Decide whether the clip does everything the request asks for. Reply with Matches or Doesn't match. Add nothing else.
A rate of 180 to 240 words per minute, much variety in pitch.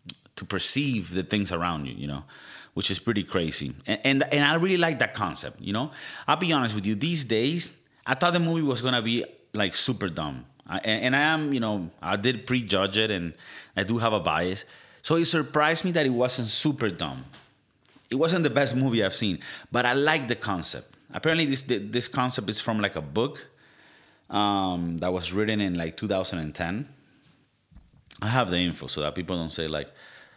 Matches